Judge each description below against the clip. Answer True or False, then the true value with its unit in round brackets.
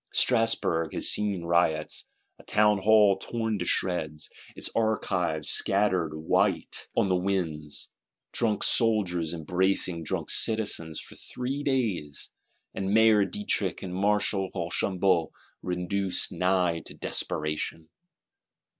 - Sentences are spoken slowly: True (110 wpm)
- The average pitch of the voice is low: True (95 Hz)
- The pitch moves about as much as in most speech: True (3.9 semitones)